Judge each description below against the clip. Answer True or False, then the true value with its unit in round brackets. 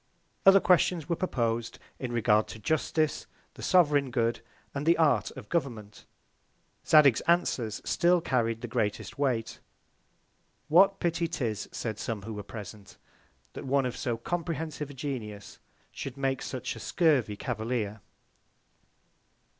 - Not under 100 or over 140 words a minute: True (135 wpm)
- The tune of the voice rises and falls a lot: True (5.9 semitones)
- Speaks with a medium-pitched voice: False (130 Hz)